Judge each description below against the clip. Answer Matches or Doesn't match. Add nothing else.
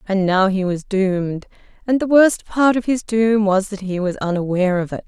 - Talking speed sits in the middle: Doesn't match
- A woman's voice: Matches